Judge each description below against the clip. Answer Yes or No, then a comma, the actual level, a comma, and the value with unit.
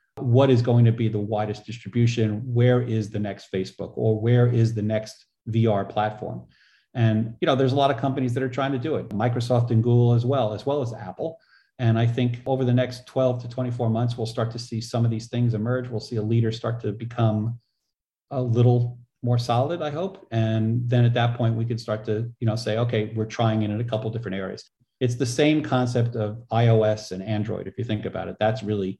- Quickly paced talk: Yes, fast, 230 wpm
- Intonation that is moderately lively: No, narrow, 2.2 semitones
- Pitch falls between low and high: No, low, 115 Hz